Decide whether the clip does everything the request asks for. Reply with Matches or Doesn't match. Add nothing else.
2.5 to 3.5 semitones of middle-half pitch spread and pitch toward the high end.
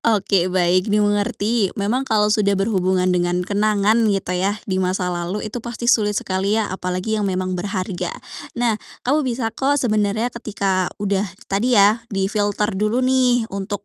Matches